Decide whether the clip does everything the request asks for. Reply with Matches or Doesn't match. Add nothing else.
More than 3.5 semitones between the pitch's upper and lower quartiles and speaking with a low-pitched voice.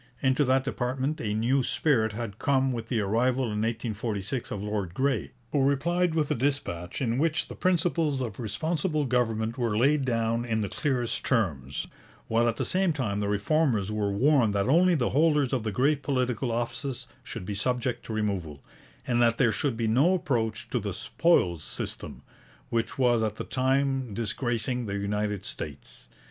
Matches